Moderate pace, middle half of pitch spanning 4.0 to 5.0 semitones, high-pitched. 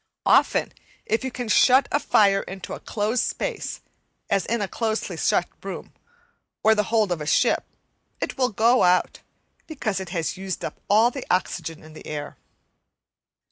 Yes: average, 170 wpm; average, 4.3 semitones; high, 210 Hz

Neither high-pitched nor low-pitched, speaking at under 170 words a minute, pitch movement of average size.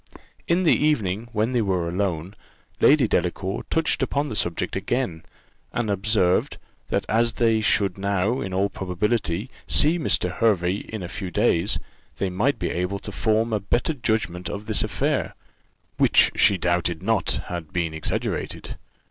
No: low, 100 Hz; average, 155 wpm; average, 4.0 semitones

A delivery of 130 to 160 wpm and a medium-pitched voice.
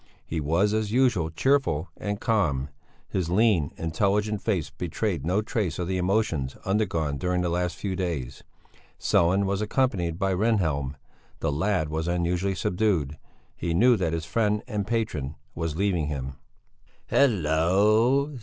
No: average, 145 wpm; very low, 90 Hz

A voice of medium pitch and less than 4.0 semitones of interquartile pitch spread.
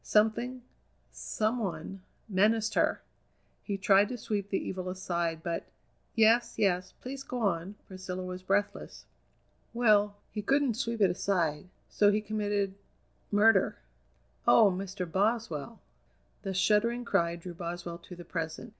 No: high, 200 Hz; average, 3.3 semitones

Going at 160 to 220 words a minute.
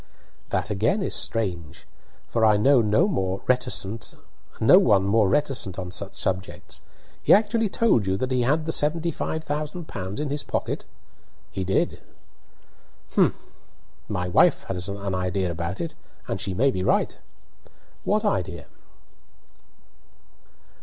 No: slow, 135 wpm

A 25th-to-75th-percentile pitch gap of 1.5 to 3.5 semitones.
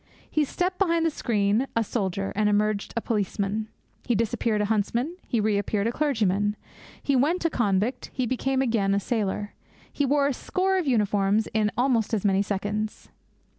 No: average, 4.6 semitones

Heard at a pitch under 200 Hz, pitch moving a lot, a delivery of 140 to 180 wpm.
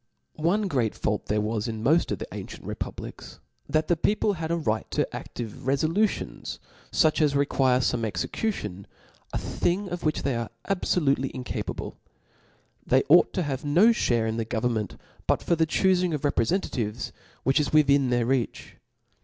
Yes: medium, 140 Hz; wide, 6.4 semitones; average, 165 wpm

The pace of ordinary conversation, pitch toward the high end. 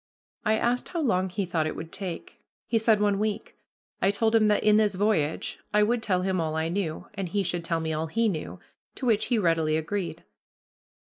No: fast, 215 wpm; high, 195 Hz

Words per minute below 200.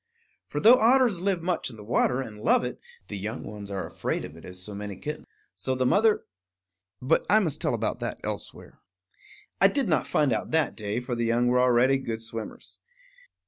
No: fast, 205 wpm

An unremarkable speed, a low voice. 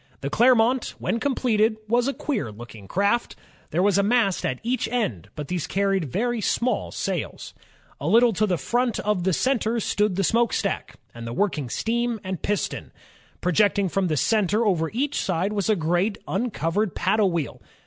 No: average, 180 wpm; high, 205 Hz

